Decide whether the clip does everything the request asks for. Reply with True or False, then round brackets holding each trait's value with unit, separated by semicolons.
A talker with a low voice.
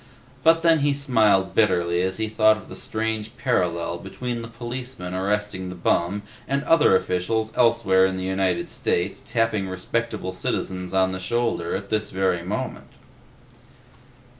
True (105 Hz)